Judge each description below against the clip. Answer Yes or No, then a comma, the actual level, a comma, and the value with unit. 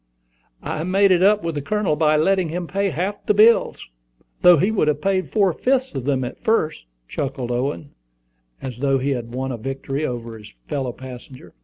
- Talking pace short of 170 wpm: No, average, 195 wpm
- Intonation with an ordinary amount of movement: No, wide, 6.7 semitones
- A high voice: No, medium, 150 Hz